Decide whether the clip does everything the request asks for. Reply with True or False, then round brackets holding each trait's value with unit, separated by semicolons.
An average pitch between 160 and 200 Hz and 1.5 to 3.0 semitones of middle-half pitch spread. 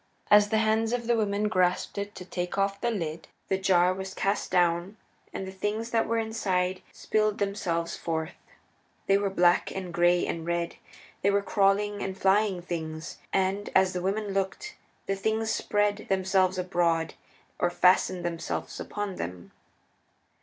True (190 Hz; 2.7 semitones)